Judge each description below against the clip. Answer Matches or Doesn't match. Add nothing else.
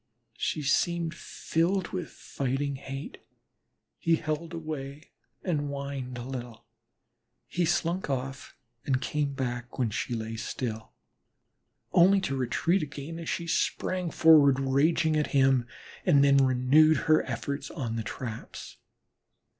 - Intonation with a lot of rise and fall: Doesn't match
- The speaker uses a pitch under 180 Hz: Matches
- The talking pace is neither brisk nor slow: Doesn't match